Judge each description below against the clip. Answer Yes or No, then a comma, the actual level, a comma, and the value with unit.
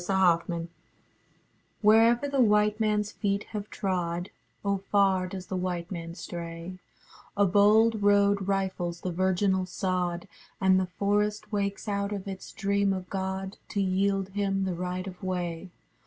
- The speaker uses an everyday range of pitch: No, narrow, 1.9 semitones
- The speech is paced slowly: No, average, 155 wpm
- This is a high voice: Yes, high, 195 Hz